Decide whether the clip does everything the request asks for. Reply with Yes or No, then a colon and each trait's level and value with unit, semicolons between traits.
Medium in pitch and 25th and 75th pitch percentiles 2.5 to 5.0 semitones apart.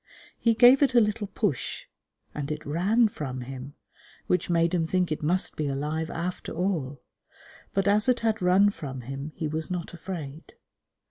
No: medium, 170 Hz; wide, 5.4 semitones